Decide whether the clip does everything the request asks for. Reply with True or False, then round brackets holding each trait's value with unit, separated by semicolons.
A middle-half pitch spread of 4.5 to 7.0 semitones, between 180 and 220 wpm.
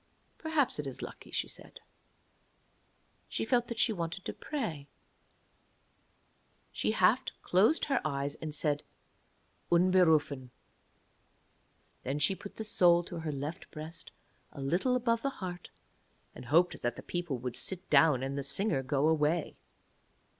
False (5.1 semitones; 140 wpm)